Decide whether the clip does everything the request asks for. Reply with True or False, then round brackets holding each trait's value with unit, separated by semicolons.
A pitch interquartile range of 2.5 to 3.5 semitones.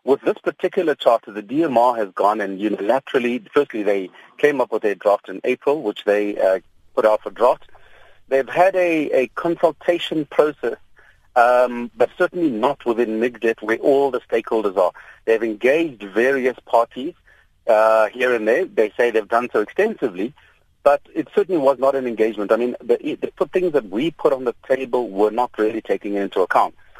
False (5.4 semitones)